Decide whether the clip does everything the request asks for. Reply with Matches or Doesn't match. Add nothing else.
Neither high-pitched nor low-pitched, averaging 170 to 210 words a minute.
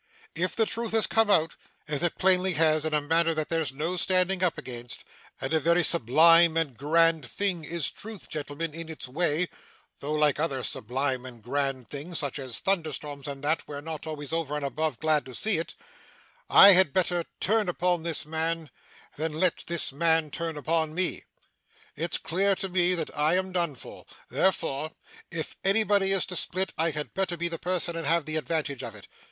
Matches